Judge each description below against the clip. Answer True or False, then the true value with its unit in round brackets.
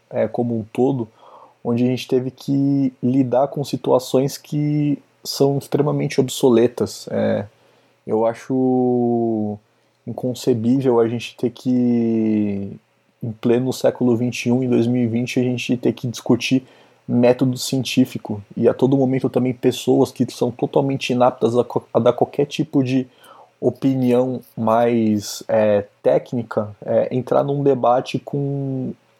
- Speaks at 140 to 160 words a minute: False (125 wpm)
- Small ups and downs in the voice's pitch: True (2.2 semitones)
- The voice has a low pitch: True (125 Hz)